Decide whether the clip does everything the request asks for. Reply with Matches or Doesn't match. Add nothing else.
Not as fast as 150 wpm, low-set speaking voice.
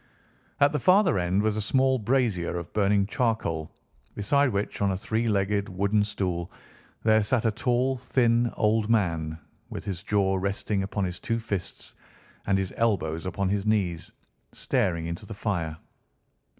Doesn't match